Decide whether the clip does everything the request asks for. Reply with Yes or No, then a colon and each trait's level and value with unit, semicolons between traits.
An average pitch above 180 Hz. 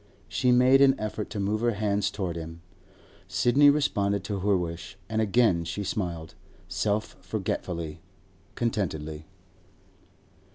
No: low, 100 Hz